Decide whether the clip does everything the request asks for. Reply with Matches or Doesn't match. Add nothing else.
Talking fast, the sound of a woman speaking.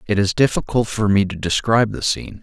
Doesn't match